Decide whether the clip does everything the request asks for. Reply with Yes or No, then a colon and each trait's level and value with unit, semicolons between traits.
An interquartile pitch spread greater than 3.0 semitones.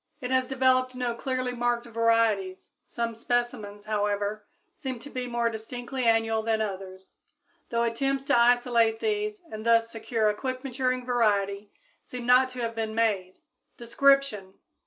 No: narrow, 2.6 semitones